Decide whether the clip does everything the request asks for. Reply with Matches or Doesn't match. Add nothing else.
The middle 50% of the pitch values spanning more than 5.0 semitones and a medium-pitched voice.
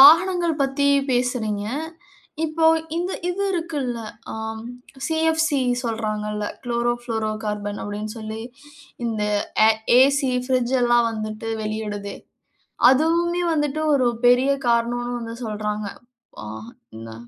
Doesn't match